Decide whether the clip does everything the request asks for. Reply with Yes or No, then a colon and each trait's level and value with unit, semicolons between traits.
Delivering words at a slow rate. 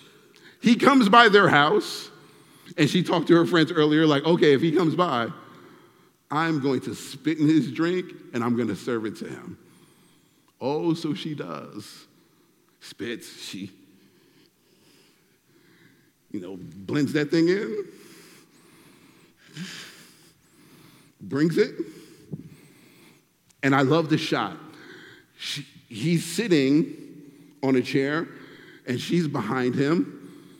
Yes: slow, 120 wpm